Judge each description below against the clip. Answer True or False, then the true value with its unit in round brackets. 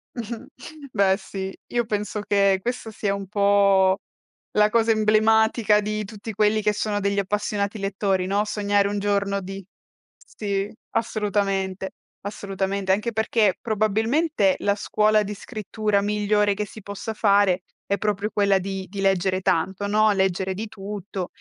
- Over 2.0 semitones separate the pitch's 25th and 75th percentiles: False (1.5 semitones)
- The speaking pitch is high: True (205 Hz)